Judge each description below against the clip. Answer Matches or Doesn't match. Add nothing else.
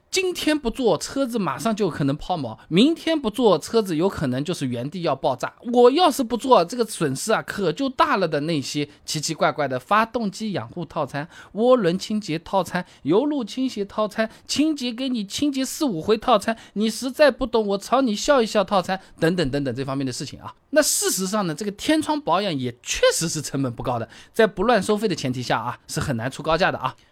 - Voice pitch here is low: Doesn't match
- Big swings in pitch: Matches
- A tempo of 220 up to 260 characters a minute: Doesn't match